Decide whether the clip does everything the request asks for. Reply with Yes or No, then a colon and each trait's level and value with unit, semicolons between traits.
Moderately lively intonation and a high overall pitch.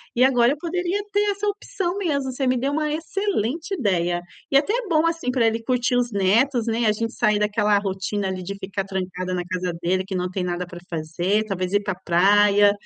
No: wide, 6.9 semitones; high, 215 Hz